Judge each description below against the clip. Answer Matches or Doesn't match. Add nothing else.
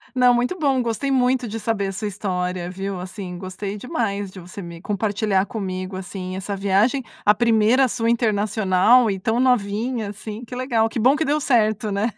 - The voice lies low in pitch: Doesn't match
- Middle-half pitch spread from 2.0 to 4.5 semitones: Matches